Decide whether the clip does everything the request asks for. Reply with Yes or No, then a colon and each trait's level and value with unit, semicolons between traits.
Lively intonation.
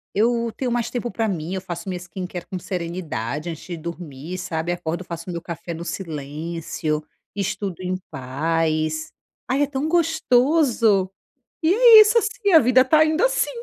Yes: wide, 7.4 semitones